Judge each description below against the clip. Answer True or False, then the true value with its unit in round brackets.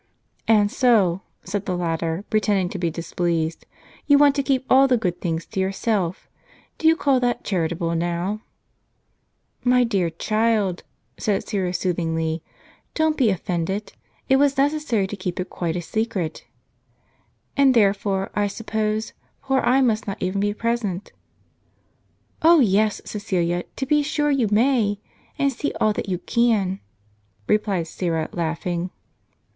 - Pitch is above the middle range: True (205 Hz)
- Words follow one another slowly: False (150 wpm)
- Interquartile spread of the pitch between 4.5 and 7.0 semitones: True (5.3 semitones)